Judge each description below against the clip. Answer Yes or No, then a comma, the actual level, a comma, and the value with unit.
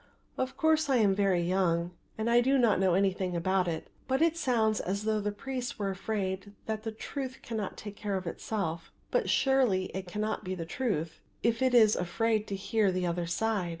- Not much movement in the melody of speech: No, average, 3.9 semitones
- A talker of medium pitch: No, high, 205 Hz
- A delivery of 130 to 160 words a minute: No, fast, 205 wpm